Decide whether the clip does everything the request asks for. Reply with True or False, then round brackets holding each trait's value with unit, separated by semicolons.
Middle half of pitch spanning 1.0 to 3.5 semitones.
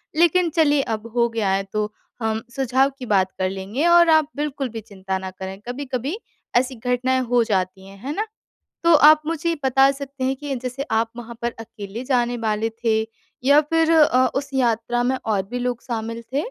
False (4.2 semitones)